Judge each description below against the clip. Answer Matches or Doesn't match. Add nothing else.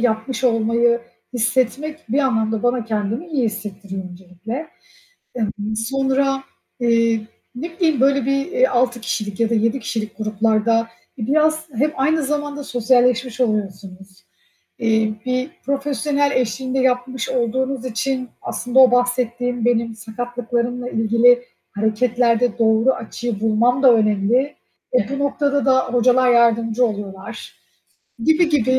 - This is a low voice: Doesn't match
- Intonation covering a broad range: Doesn't match